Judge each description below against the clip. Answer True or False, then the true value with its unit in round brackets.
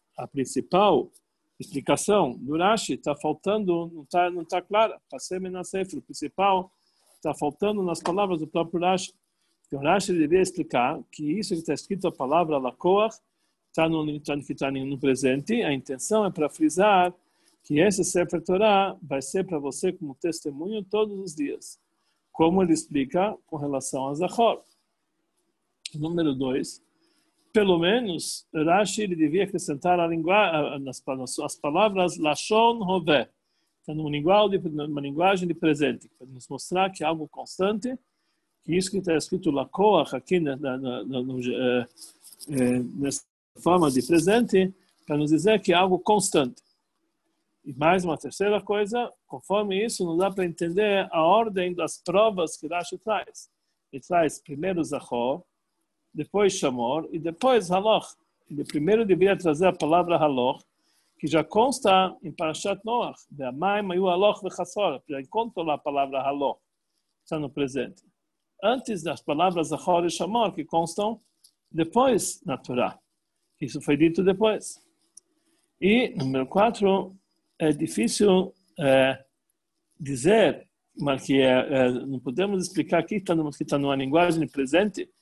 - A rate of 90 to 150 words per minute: True (140 wpm)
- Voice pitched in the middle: True (175 Hz)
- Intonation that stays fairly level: False (5.1 semitones)